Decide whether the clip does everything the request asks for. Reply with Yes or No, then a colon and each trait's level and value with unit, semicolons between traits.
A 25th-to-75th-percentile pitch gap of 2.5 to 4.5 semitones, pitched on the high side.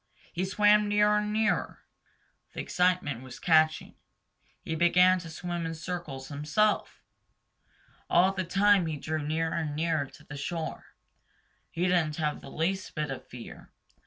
No: average, 3.3 semitones; medium, 170 Hz